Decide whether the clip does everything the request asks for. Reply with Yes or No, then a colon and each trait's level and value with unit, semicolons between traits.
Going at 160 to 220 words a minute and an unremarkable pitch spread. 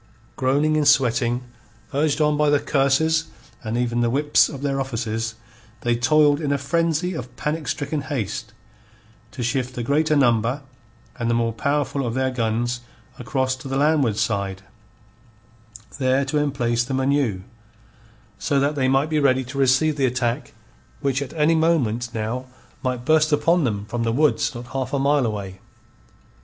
Yes: average, 165 wpm; average, 3.5 semitones